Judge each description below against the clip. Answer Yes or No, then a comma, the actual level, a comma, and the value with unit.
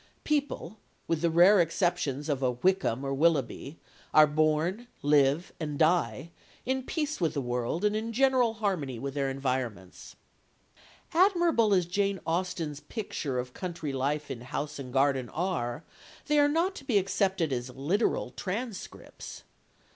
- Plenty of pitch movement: Yes, wide, 6.8 semitones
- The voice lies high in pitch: No, medium, 165 Hz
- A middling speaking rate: Yes, average, 150 wpm